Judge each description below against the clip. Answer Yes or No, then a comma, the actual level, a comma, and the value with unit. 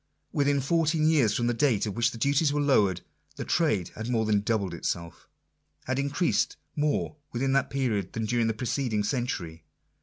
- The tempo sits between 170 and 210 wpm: Yes, average, 185 wpm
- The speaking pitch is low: Yes, low, 120 Hz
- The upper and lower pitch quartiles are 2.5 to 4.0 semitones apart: No, average, 4.9 semitones